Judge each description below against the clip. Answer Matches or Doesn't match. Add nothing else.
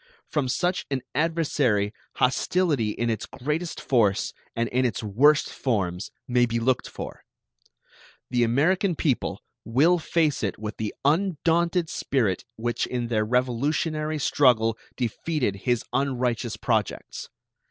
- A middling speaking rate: Doesn't match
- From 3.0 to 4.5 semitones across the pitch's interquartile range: Doesn't match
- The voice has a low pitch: Matches